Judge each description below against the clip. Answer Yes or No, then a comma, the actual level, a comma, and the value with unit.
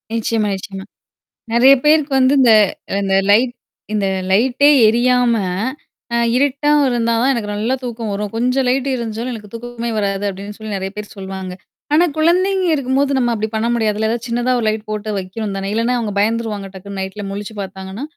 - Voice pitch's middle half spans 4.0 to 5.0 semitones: No, average, 3.5 semitones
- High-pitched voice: Yes, high, 225 Hz